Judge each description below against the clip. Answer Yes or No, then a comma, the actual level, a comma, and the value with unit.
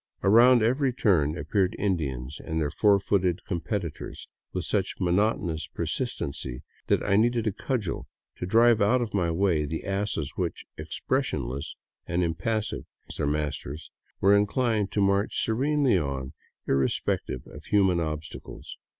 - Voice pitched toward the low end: Yes, very low, 95 Hz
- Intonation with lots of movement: Yes, wide, 5.8 semitones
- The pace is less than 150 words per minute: Yes, average, 140 wpm